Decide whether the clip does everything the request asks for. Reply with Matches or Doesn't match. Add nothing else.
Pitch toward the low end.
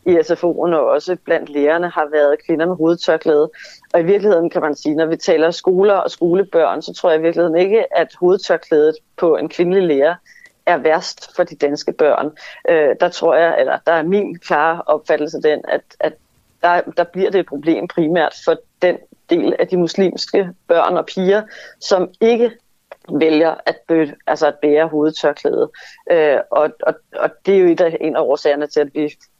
Doesn't match